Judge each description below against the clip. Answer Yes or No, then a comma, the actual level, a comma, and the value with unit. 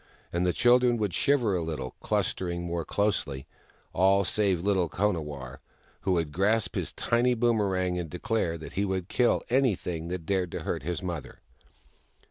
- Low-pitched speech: Yes, very low, 95 Hz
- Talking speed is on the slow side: No, average, 165 wpm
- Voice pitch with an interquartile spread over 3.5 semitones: Yes, average, 3.9 semitones